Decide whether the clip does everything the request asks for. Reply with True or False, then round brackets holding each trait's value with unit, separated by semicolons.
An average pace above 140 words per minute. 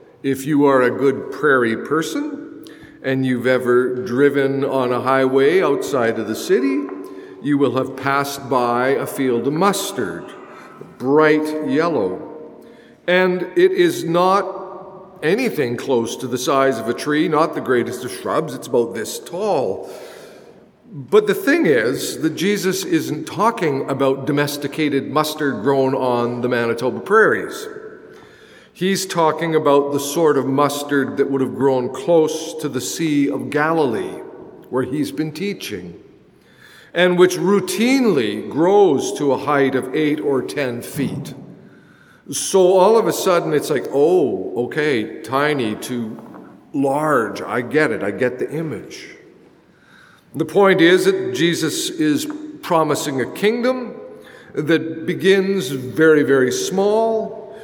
False (135 wpm)